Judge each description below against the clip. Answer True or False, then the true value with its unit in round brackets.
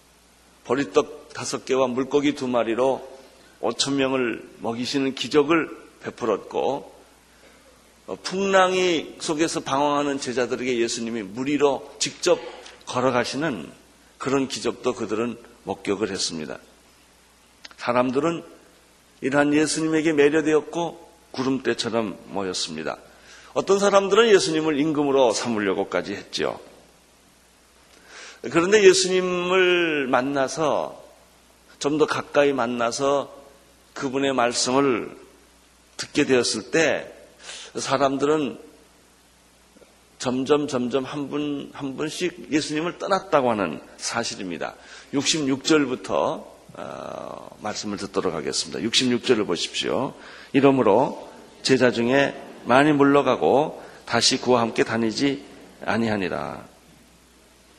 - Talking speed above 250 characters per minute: False (240 characters per minute)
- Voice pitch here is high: False (135 Hz)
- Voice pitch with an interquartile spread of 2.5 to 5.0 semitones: True (3.8 semitones)